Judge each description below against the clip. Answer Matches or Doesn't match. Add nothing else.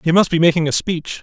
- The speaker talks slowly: Doesn't match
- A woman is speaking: Doesn't match